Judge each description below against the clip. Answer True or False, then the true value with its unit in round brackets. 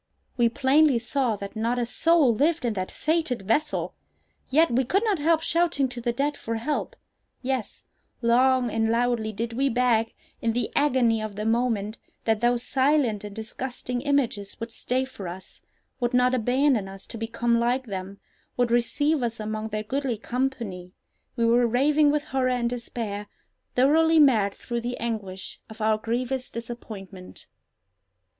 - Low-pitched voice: False (240 Hz)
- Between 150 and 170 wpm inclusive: True (160 wpm)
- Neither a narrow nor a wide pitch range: True (3.1 semitones)